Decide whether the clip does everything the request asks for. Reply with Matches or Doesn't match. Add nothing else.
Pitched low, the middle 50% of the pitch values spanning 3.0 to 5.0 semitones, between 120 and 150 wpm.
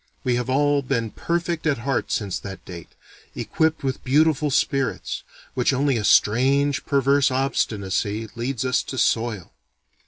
Matches